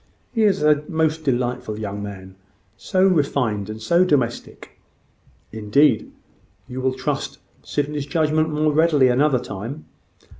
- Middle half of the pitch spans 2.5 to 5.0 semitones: No, wide, 5.6 semitones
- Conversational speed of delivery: No, slow, 125 wpm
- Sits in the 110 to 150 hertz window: Yes, medium, 140 Hz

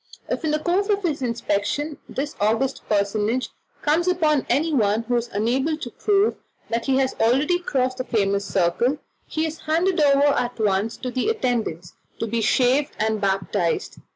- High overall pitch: Yes, very high, 255 Hz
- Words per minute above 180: No, average, 170 wpm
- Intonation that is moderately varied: No, wide, 5.7 semitones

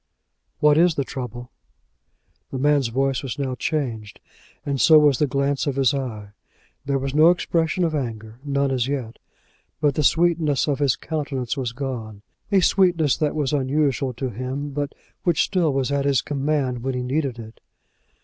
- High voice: No, medium, 140 Hz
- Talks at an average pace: Yes, average, 175 wpm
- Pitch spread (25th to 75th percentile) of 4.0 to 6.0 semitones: No, average, 2.8 semitones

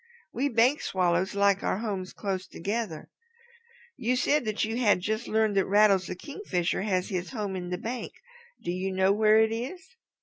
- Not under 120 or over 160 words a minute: No, average, 180 wpm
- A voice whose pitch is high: Yes, high, 205 Hz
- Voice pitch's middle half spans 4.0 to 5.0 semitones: No, average, 3.4 semitones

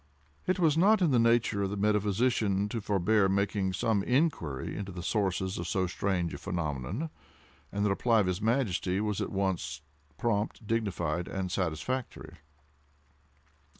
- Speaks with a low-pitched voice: Yes, low, 100 Hz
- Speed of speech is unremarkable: Yes, average, 150 wpm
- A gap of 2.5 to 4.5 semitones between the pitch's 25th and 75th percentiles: Yes, average, 3.7 semitones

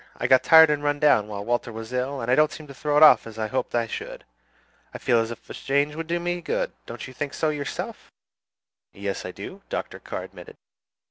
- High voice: No, medium, 140 Hz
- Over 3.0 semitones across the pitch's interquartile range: Yes, average, 4.9 semitones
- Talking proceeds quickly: Yes, fast, 240 wpm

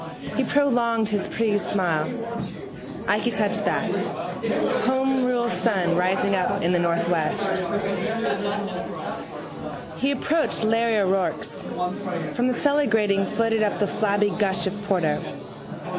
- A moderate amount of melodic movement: Yes, average, 4.0 semitones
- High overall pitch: Yes, high, 210 Hz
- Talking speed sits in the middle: No, slow, 115 wpm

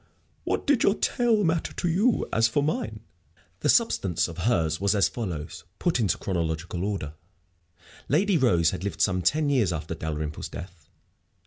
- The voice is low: Yes, low, 100 Hz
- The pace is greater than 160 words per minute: Yes, average, 170 wpm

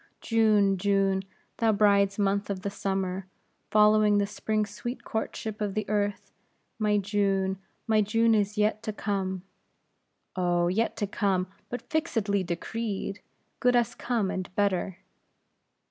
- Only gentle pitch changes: Yes, narrow, 1.8 semitones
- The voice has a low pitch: No, high, 205 Hz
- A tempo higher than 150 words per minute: No, slow, 135 wpm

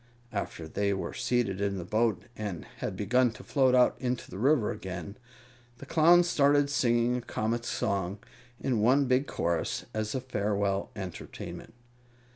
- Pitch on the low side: Yes, low, 110 Hz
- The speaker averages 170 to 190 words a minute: No, average, 155 wpm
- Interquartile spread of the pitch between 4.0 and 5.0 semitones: Yes, average, 4.3 semitones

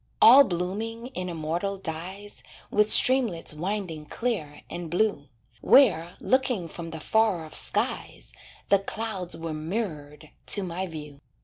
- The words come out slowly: Yes, slow, 130 wpm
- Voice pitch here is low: No, medium, 180 Hz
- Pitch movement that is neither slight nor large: Yes, average, 4.8 semitones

